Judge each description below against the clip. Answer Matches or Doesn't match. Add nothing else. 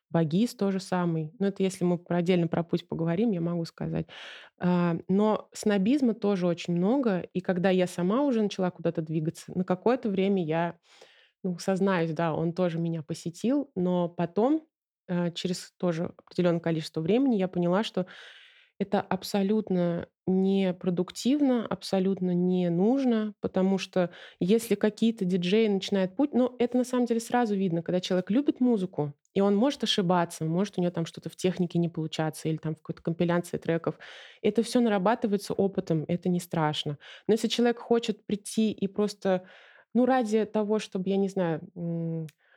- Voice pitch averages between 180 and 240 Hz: Matches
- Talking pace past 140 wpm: Matches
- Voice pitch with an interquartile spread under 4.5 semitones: Matches